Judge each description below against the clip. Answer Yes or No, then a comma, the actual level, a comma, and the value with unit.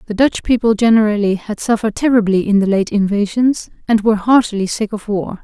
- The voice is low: No, high, 215 Hz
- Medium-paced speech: Yes, average, 190 wpm